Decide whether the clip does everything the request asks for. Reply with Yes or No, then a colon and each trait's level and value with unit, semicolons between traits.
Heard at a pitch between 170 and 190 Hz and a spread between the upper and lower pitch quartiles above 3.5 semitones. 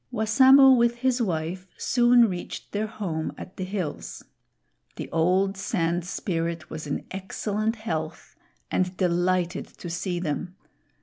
Yes: medium, 185 Hz; average, 4.3 semitones